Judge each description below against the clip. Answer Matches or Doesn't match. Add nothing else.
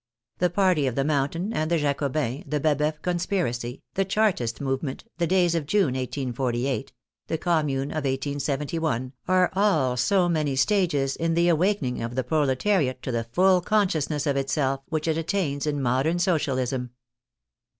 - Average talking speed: Matches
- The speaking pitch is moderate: Matches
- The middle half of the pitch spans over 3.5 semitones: Matches